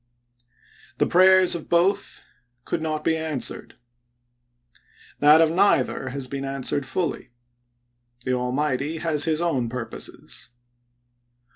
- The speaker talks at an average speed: No, slow, 115 wpm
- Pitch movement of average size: Yes, average, 4.1 semitones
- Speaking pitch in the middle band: Yes, medium, 150 Hz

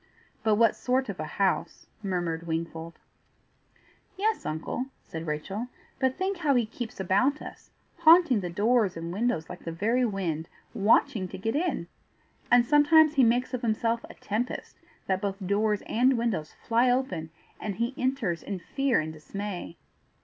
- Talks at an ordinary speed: Yes, average, 160 wpm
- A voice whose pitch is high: Yes, high, 215 Hz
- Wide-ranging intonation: Yes, wide, 6.0 semitones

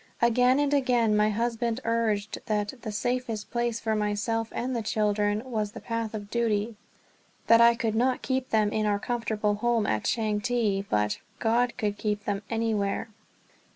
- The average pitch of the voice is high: Yes, high, 225 Hz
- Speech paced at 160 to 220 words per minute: Yes, average, 165 wpm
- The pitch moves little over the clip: Yes, narrow, 2.2 semitones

